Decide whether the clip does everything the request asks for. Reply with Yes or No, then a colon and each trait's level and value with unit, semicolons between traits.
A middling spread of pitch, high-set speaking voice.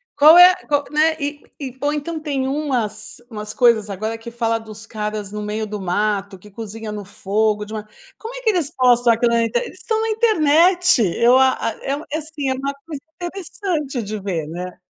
No: wide, 6.1 semitones; high, 245 Hz